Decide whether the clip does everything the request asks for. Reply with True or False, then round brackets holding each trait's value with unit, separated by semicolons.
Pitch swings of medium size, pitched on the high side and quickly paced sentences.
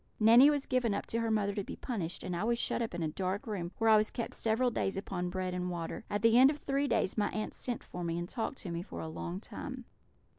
True (4.7 semitones; 210 Hz; 275 wpm)